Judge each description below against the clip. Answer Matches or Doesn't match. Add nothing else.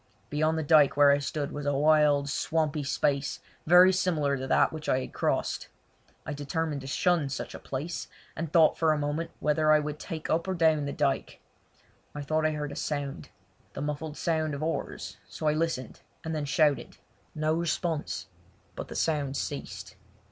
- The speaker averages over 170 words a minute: Matches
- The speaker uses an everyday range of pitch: Doesn't match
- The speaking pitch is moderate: Matches